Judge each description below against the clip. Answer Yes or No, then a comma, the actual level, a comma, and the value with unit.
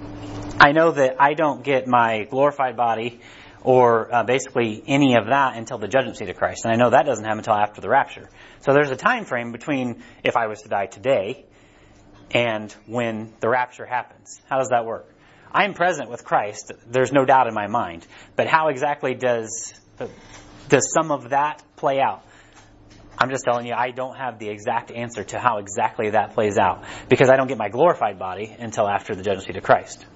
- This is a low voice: Yes, low, 120 Hz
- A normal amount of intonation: Yes, average, 3.5 semitones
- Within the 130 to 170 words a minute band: No, fast, 205 wpm